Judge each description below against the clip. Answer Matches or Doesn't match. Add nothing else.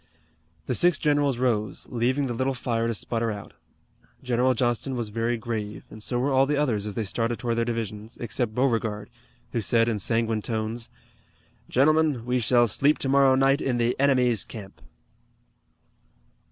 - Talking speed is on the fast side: Doesn't match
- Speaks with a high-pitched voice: Doesn't match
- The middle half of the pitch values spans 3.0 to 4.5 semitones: Doesn't match